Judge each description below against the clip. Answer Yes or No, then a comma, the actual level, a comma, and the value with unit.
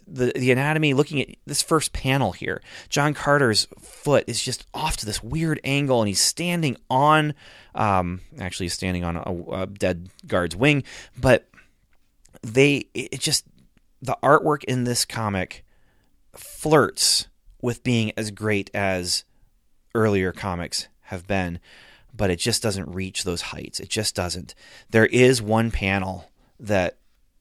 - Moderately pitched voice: No, low, 110 Hz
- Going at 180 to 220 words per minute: No, average, 145 wpm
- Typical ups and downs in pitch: No, wide, 6.3 semitones